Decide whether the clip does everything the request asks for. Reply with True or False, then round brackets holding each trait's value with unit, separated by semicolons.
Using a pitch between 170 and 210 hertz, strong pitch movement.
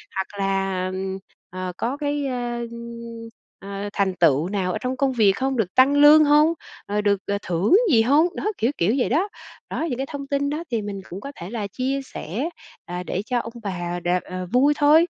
False (225 Hz; 6.6 semitones)